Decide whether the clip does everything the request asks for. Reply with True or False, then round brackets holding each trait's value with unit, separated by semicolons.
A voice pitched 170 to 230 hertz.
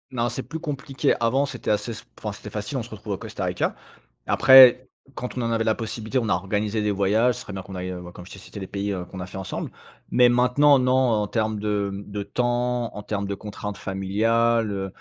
False (110 Hz)